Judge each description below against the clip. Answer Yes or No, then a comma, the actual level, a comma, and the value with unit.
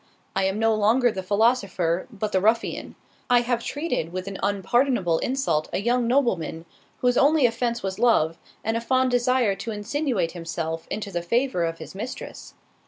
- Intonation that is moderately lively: Yes, average, 5.0 semitones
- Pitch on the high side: Yes, high, 220 Hz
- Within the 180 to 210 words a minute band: No, average, 170 wpm